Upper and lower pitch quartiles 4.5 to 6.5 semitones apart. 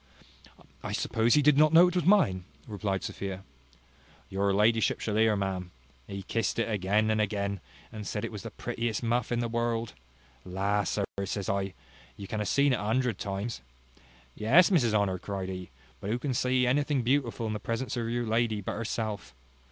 No: average, 3.2 semitones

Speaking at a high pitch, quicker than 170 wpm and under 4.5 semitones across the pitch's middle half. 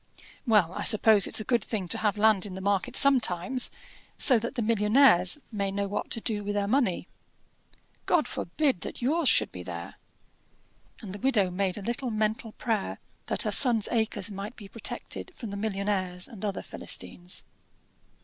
Yes: high, 210 Hz; average, 180 wpm; average, 3.3 semitones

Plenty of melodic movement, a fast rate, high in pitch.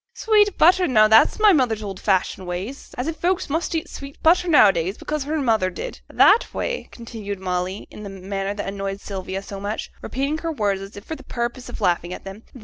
Yes: wide, 7.9 semitones; fast, 225 wpm; high, 215 Hz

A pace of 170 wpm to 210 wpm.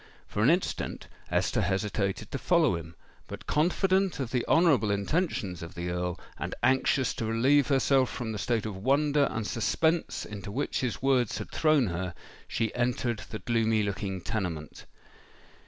No: average, 160 wpm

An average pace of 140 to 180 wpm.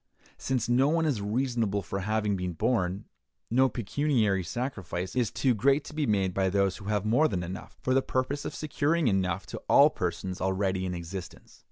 No: average, 190 wpm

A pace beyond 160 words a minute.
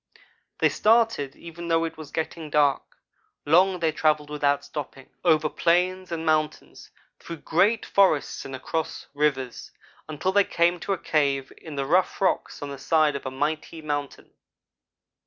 No: average, 155 wpm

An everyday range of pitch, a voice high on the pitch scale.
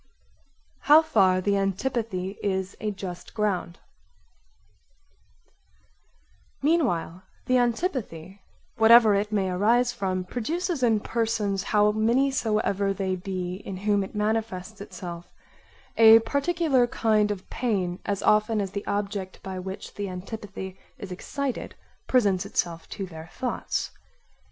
Yes: average, 3.4 semitones; high, 205 Hz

